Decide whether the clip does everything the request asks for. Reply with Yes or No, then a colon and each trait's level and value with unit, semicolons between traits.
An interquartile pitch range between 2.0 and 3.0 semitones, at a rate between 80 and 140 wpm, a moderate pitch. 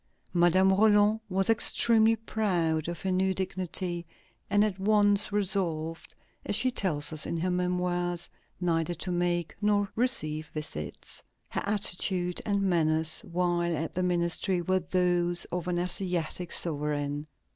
Yes: narrow, 2.4 semitones; slow, 135 wpm; medium, 180 Hz